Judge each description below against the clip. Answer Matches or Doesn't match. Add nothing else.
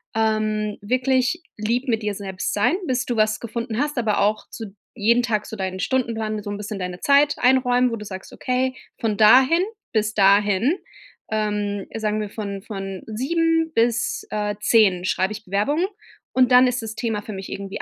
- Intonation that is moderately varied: Matches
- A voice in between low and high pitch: Doesn't match